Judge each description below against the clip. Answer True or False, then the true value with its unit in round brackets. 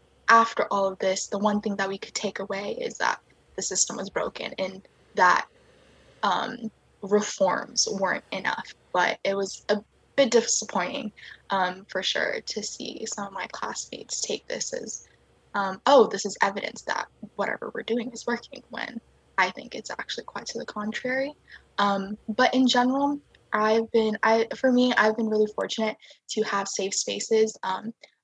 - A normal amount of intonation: True (3.4 semitones)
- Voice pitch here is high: True (215 Hz)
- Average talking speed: True (170 wpm)